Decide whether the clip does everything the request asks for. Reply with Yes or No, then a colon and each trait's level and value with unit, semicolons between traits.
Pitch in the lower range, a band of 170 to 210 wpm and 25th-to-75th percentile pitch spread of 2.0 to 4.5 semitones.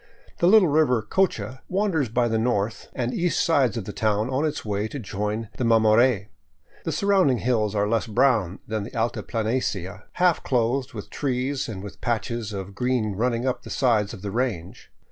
Yes: low, 115 Hz; average, 185 wpm; average, 3.7 semitones